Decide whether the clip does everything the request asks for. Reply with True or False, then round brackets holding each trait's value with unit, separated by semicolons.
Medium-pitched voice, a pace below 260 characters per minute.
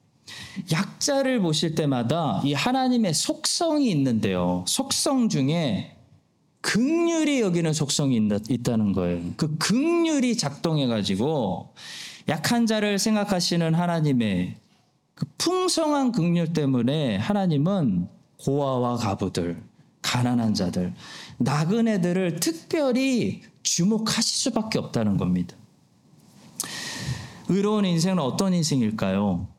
True (170 Hz; 245 characters per minute)